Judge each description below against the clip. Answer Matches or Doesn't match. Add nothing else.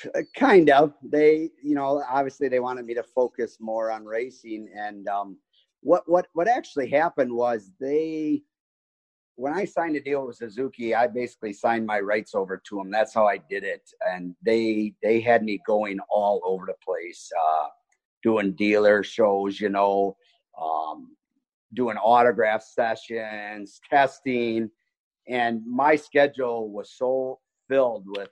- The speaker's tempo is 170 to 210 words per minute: Doesn't match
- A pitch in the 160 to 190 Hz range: Doesn't match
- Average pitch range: Doesn't match